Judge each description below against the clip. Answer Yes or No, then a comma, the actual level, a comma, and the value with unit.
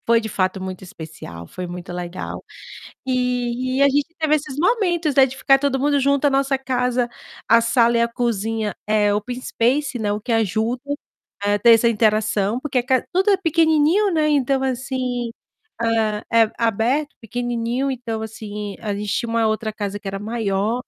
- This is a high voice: Yes, high, 235 Hz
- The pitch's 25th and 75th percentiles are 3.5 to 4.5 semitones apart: Yes, average, 4.0 semitones